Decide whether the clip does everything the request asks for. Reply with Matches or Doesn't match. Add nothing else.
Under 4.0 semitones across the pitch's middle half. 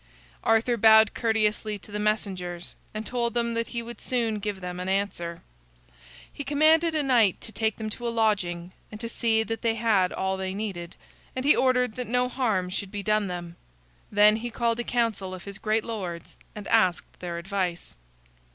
Matches